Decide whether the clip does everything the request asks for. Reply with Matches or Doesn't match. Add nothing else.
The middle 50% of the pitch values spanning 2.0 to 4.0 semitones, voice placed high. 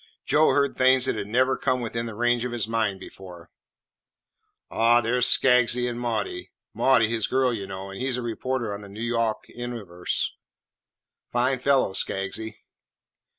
Doesn't match